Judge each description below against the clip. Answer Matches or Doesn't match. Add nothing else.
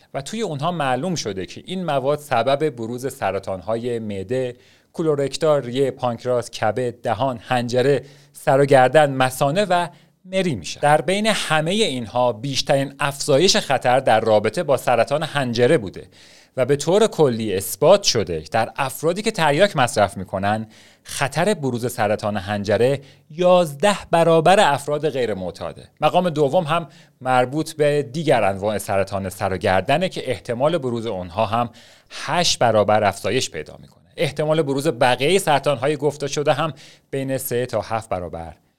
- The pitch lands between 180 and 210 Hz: Doesn't match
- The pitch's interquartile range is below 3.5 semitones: Doesn't match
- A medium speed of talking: Matches